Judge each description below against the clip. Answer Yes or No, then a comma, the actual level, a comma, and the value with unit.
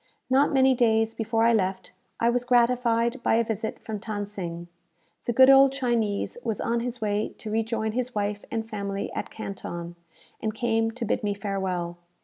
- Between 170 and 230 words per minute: Yes, average, 180 wpm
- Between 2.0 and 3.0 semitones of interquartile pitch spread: Yes, average, 2.7 semitones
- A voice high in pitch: Yes, high, 225 Hz